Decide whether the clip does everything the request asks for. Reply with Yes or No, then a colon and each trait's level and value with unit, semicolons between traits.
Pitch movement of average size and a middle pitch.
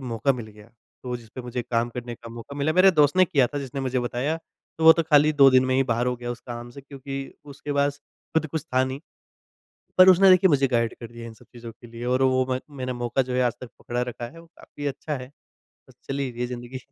No: average, 3.0 semitones; low, 130 Hz